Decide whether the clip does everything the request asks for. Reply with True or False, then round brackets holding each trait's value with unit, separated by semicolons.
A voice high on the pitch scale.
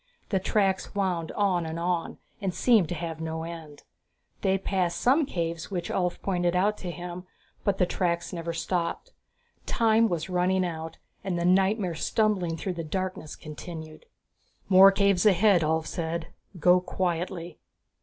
False (180 Hz)